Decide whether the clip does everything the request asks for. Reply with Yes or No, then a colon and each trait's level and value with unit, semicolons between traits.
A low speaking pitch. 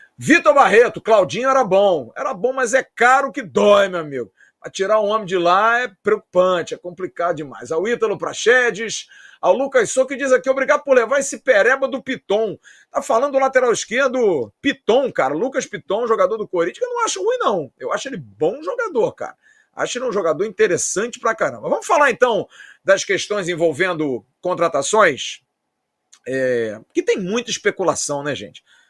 No: high, 235 Hz